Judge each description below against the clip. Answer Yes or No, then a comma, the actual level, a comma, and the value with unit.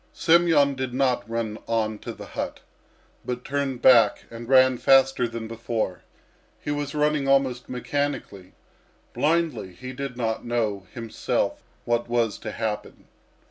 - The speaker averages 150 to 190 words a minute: No, average, 140 wpm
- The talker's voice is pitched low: Yes, low, 125 Hz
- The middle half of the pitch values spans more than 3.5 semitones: No, average, 3.2 semitones